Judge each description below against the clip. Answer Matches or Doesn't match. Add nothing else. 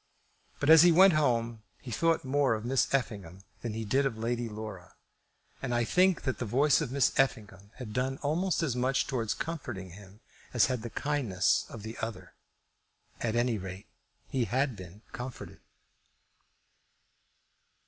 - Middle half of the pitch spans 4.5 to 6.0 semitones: Doesn't match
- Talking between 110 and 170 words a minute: Matches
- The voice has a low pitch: Matches